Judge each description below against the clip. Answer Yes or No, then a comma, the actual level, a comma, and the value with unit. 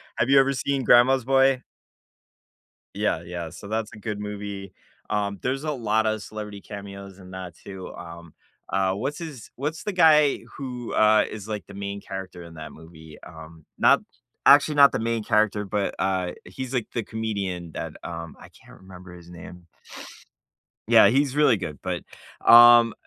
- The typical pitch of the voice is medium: No, low, 105 Hz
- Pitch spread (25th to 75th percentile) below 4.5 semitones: No, average, 4.9 semitones